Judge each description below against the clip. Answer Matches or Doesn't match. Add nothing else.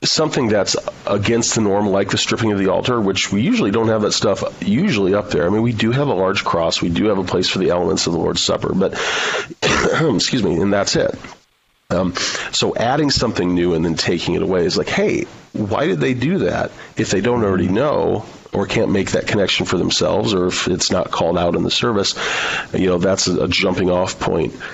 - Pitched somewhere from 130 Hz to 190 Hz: Doesn't match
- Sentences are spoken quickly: Matches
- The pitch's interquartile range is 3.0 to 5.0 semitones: Matches